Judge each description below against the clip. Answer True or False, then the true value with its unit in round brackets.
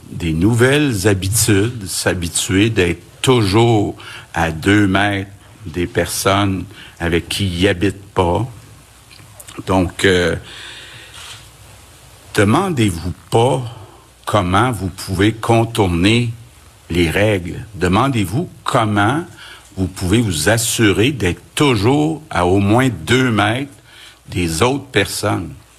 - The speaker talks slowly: True (100 wpm)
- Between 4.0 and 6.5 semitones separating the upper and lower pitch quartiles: False (3.5 semitones)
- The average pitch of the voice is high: False (105 Hz)